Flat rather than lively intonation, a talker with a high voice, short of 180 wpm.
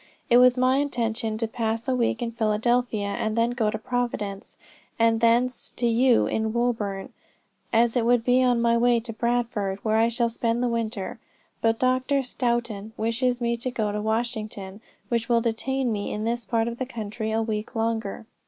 No: narrow, 1.7 semitones; high, 230 Hz; average, 190 wpm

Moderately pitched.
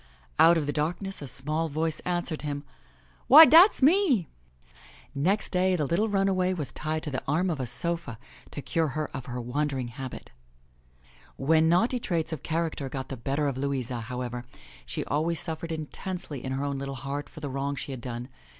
Yes: medium, 150 Hz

